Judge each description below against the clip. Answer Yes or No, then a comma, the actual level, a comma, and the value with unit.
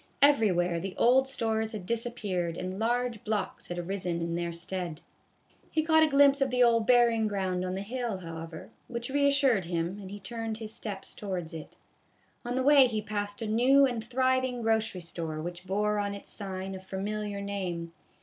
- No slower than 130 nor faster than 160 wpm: No, average, 185 wpm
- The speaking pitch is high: Yes, high, 210 Hz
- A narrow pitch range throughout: No, average, 4.8 semitones